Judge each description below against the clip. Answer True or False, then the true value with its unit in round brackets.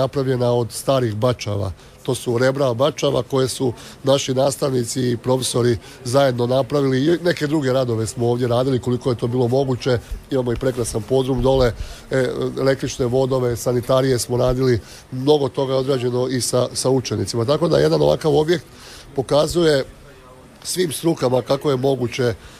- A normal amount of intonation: False (1.9 semitones)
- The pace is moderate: True (150 wpm)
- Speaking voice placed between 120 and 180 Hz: True (130 Hz)